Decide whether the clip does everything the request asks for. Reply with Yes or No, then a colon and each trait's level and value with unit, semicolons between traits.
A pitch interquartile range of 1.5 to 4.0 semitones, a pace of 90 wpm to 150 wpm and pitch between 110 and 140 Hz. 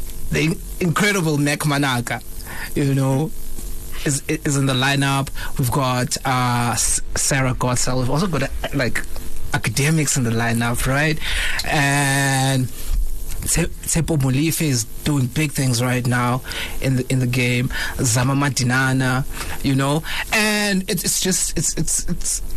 Yes: average, 3.4 semitones; slow, 135 wpm; low, 135 Hz